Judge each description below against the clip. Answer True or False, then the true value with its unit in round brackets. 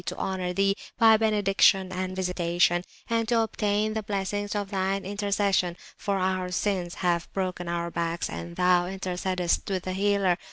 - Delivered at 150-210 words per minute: True (160 wpm)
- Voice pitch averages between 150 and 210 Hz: True (190 Hz)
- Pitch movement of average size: False (2.2 semitones)